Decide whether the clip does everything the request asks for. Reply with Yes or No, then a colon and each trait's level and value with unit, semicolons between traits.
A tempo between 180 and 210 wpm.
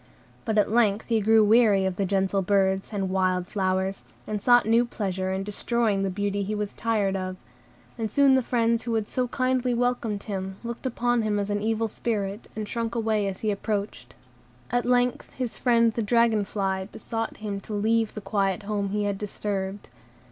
Yes: average, 190 wpm